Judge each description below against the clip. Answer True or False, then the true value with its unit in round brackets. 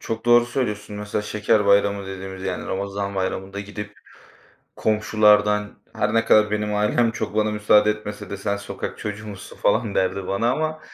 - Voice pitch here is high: False (105 Hz)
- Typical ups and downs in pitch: False (1.1 semitones)